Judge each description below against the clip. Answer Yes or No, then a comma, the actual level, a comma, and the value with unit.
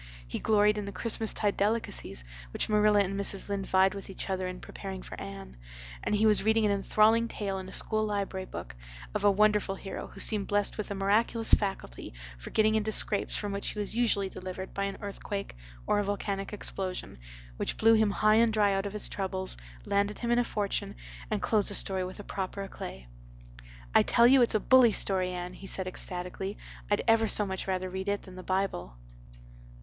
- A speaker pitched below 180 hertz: No, high, 200 Hz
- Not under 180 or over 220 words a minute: Yes, fast, 205 wpm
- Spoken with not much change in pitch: Yes, narrow, 1.9 semitones